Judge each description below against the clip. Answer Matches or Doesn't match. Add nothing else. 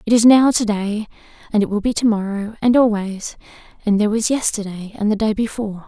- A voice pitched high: Matches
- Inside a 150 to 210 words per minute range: Matches